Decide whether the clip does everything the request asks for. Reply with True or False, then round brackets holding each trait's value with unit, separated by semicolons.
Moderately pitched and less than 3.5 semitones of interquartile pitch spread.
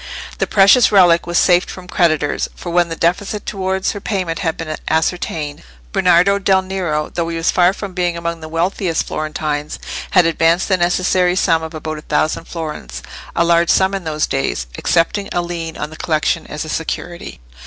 True (170 Hz; 2.6 semitones)